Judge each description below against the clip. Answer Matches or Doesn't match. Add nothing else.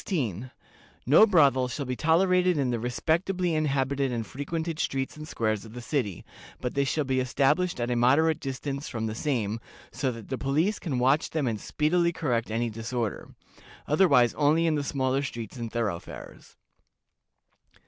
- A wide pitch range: Doesn't match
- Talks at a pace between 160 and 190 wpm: Matches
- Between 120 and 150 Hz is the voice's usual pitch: Matches